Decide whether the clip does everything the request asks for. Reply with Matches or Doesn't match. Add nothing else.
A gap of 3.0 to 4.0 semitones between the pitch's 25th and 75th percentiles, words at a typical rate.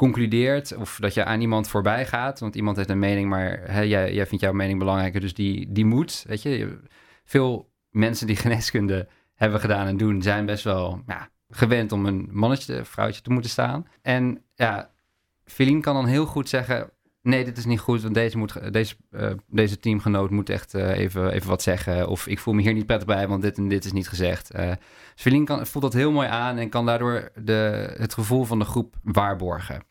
Doesn't match